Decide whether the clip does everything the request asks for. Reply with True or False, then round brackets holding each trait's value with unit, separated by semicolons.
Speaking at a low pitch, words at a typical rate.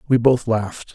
True (115 Hz; 190 wpm)